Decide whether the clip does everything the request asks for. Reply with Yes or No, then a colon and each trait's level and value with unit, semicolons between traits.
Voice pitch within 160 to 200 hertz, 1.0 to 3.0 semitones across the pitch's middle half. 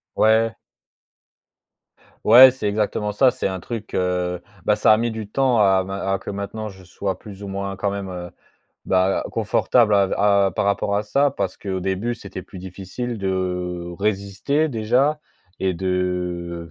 No: low, 100 Hz; average, 2.7 semitones